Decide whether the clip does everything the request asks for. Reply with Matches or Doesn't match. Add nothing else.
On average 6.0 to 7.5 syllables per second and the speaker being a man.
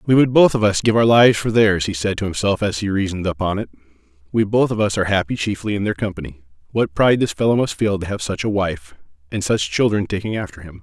Matches